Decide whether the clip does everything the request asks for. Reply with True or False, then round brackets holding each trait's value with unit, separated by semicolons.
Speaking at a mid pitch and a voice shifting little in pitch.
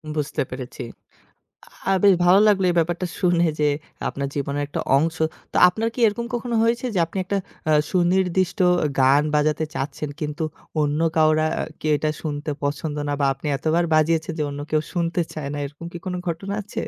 False (160 Hz; 3.7 semitones)